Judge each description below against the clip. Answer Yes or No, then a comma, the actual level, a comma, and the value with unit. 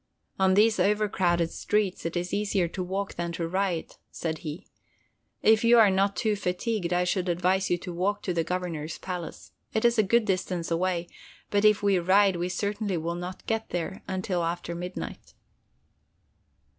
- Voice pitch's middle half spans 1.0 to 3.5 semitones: Yes, average, 2.7 semitones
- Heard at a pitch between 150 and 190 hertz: Yes, medium, 185 Hz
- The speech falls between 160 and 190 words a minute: Yes, average, 175 wpm